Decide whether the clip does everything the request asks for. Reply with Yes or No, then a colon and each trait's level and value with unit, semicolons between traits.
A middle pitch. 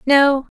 No: very high, 275 Hz